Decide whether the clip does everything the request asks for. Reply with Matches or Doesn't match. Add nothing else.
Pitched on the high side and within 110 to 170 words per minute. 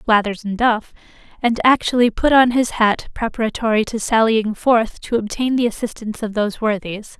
Matches